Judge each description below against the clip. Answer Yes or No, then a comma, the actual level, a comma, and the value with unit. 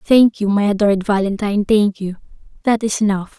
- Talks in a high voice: Yes, high, 205 Hz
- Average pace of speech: Yes, average, 175 wpm